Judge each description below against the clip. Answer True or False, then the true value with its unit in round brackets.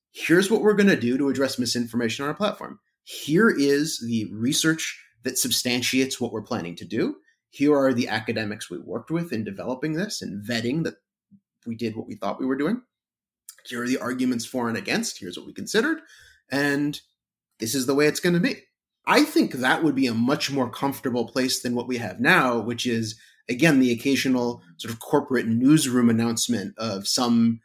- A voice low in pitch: True (125 Hz)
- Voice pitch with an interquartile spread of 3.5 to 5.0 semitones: True (3.9 semitones)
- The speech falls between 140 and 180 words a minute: False (195 wpm)